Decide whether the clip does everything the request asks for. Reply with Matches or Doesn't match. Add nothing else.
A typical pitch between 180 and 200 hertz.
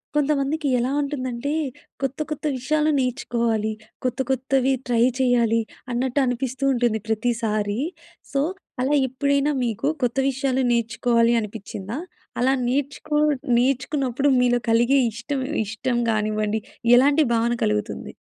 Doesn't match